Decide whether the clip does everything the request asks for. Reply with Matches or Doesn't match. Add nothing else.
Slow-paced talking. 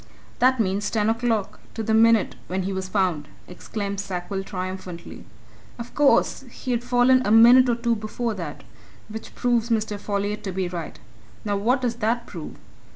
Doesn't match